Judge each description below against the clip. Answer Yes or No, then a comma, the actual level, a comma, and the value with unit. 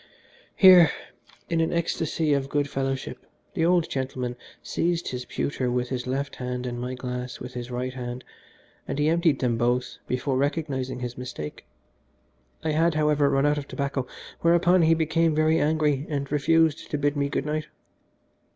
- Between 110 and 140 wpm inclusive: No, average, 170 wpm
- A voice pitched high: No, medium, 140 Hz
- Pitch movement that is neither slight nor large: Yes, average, 4.0 semitones